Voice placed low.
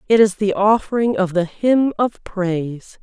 No: high, 205 Hz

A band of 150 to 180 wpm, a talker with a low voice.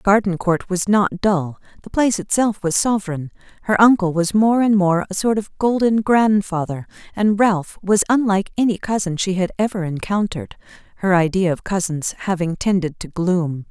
No: average, 160 wpm; high, 195 Hz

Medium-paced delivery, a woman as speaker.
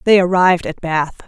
Yes: average, 190 wpm; female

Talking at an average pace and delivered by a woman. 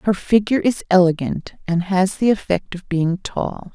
Yes: average, 175 wpm; female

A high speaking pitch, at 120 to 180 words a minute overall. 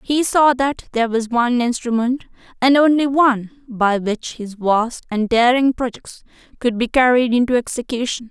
Yes: high, 245 Hz; average, 160 wpm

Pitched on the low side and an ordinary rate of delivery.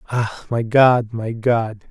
Yes: low, 115 Hz; average, 155 wpm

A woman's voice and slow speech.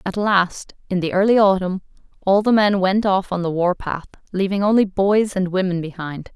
No: female; average, 200 wpm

